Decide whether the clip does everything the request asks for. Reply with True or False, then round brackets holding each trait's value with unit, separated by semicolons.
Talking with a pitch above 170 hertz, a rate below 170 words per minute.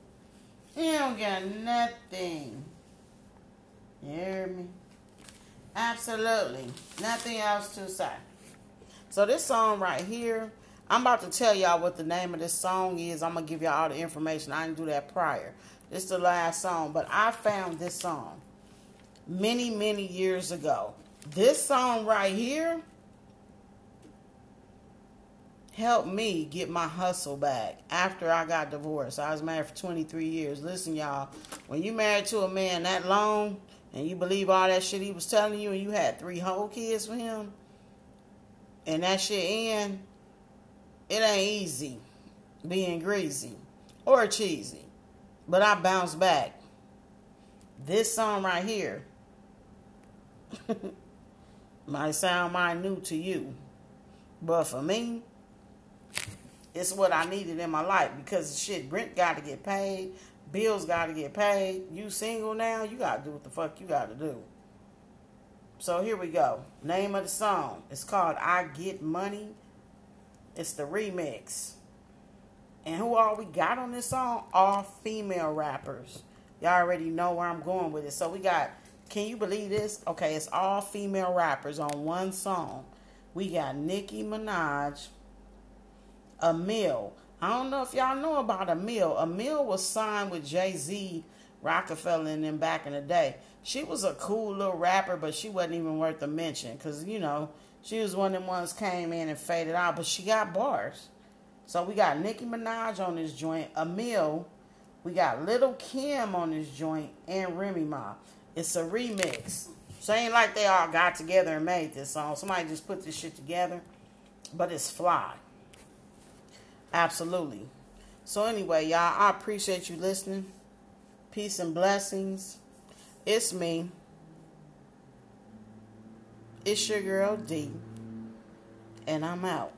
True (185 Hz; 155 wpm)